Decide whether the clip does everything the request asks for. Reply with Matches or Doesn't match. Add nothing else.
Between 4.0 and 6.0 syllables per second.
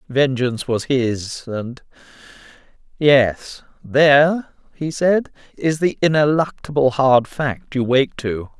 Doesn't match